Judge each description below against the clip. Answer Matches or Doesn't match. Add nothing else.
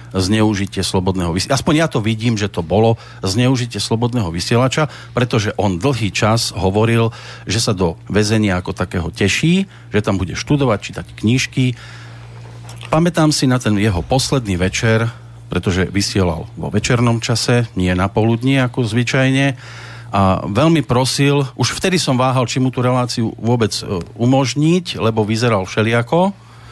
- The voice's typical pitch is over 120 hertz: Doesn't match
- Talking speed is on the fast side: Doesn't match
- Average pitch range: Matches